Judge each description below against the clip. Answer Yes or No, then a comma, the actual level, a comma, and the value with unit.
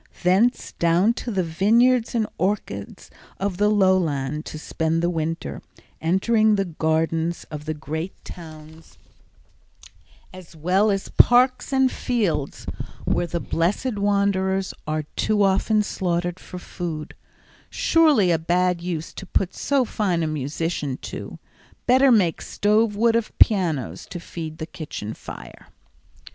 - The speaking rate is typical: No, slow, 130 wpm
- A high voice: No, medium, 180 Hz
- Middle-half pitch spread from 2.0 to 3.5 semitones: No, average, 4.6 semitones